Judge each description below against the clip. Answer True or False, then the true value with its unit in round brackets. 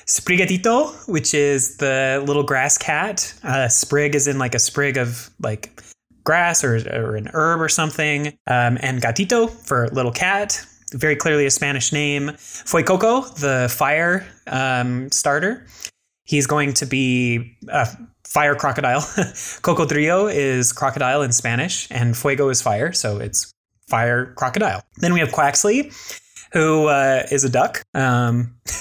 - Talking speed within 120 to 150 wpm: True (145 wpm)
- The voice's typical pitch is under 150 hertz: True (140 Hz)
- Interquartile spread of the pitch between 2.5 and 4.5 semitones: True (4.0 semitones)